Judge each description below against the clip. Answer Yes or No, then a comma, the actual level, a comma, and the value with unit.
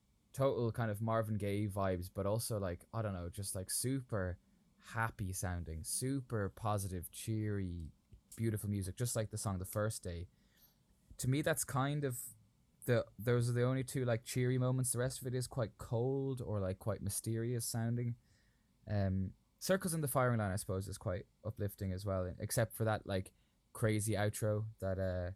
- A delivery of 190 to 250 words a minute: No, average, 180 wpm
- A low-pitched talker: Yes, low, 110 Hz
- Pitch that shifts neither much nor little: Yes, average, 3.8 semitones